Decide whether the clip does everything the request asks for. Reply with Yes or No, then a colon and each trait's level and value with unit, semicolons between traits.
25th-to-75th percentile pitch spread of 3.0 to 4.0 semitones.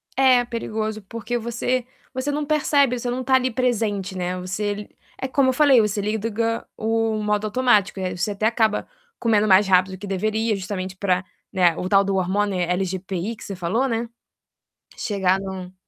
Yes: average, 3.7 semitones